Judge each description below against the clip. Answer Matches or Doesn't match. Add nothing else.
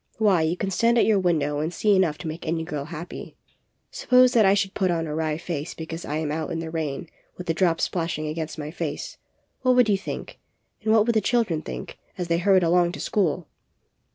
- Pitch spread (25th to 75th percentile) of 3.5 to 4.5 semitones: Matches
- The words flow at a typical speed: Doesn't match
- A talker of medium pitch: Matches